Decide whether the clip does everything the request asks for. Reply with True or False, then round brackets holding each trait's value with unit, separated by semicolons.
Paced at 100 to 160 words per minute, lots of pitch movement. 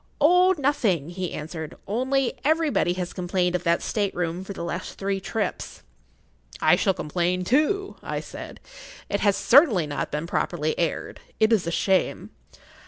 True (155 wpm; 6.6 semitones)